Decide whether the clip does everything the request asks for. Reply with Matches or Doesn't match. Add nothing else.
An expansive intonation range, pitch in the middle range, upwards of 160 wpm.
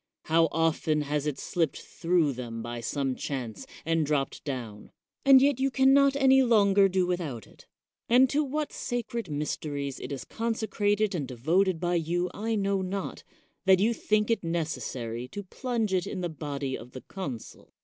Matches